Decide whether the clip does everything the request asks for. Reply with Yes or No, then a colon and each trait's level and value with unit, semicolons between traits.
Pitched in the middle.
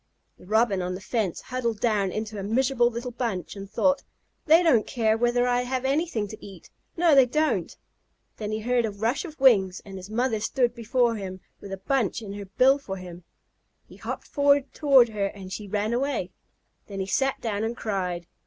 No: high, 225 Hz